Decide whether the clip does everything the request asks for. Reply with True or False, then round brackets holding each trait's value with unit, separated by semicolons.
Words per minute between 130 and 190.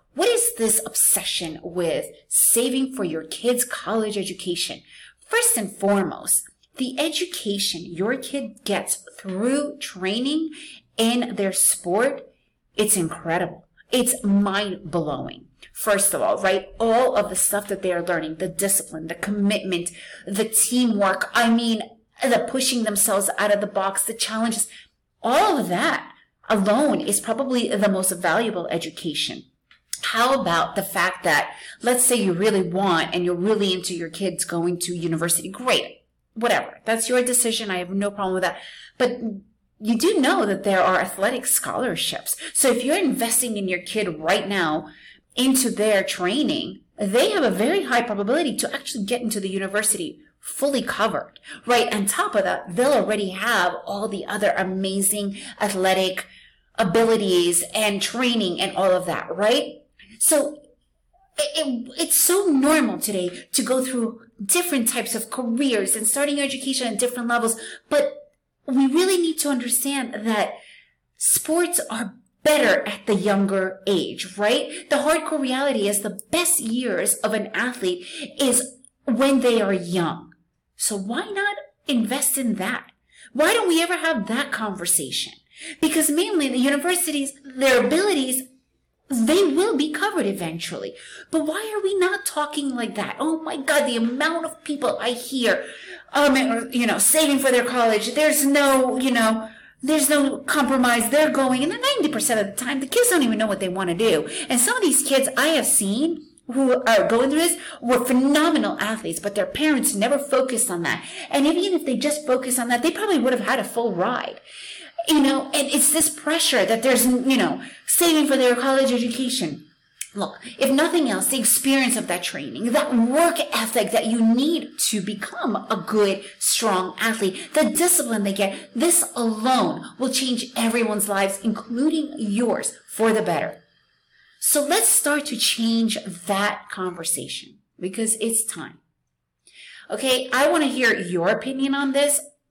True (165 wpm)